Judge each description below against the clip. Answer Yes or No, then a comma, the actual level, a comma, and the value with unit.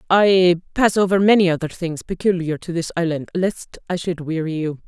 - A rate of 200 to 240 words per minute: No, average, 185 wpm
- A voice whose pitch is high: No, medium, 175 Hz